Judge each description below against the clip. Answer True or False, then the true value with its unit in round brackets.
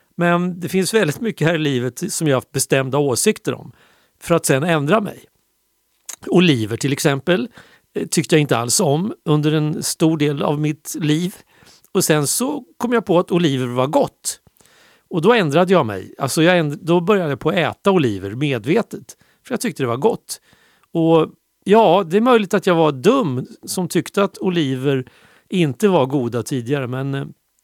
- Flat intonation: False (4.7 semitones)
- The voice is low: False (165 Hz)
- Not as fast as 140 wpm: False (185 wpm)